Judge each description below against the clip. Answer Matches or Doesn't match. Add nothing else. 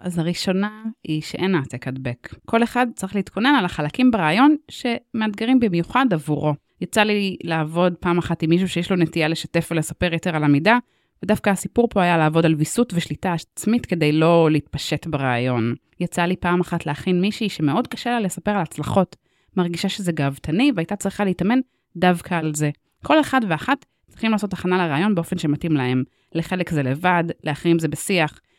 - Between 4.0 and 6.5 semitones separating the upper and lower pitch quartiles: Matches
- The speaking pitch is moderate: Matches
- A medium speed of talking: Doesn't match